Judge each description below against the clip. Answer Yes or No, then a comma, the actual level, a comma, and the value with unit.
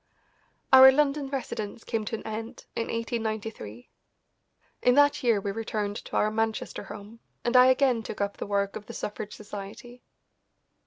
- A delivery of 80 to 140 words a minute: No, average, 160 wpm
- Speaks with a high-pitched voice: Yes, high, 225 Hz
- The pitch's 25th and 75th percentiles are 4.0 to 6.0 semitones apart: No, average, 3.2 semitones